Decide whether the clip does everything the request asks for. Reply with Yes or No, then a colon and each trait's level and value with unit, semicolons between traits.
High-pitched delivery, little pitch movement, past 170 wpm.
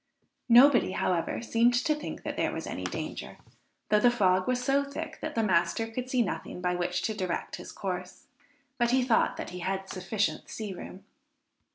No: high, 215 Hz; average, 5.1 semitones; average, 190 wpm